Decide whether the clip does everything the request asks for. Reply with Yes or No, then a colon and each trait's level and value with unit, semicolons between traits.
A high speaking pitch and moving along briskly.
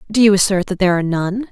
Yes: high, 195 Hz; fast, 275 wpm